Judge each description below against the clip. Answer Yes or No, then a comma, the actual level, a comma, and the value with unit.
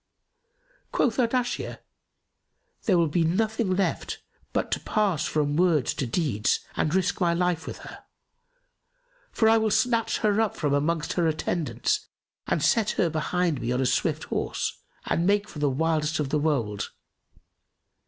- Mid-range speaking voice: Yes, medium, 170 Hz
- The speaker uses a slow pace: No, average, 155 wpm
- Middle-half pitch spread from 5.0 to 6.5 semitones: Yes, wide, 5.5 semitones